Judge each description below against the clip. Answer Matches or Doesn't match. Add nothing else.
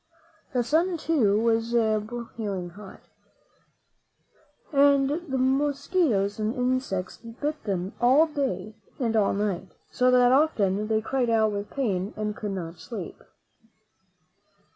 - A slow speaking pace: Matches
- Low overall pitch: Doesn't match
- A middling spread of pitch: Matches